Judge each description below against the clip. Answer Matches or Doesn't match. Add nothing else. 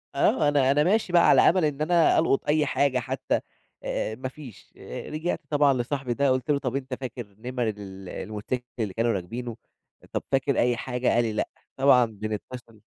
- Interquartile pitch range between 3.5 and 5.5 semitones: Matches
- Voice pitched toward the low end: Matches